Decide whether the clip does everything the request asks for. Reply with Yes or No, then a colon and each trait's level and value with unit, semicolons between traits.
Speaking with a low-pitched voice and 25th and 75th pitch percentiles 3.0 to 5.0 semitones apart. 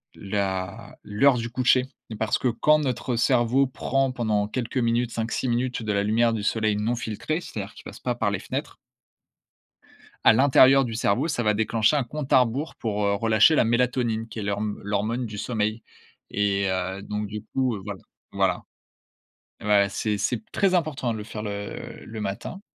Yes: low, 115 Hz; average, 3.3 semitones